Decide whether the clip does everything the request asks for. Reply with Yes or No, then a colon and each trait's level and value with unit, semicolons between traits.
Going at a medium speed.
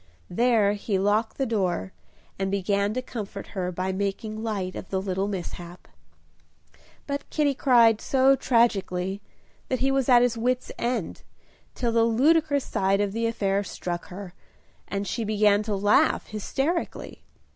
Yes: average, 150 wpm